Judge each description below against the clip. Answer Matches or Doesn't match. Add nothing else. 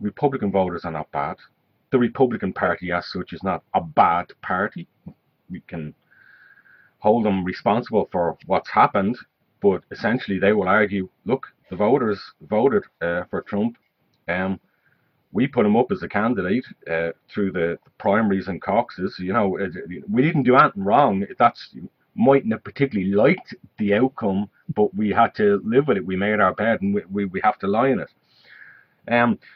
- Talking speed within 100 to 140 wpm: Doesn't match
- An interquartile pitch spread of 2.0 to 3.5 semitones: Matches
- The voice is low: Matches